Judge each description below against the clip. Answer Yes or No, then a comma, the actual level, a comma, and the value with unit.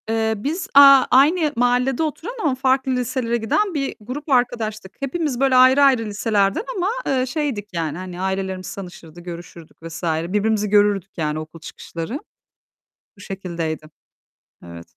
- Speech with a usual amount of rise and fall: No, wide, 6.5 semitones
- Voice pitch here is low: No, high, 220 Hz